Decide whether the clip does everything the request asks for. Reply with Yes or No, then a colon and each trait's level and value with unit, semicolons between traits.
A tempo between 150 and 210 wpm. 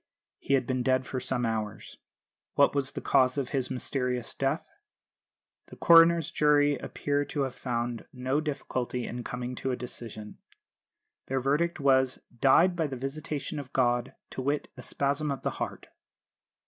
Yes: average, 160 wpm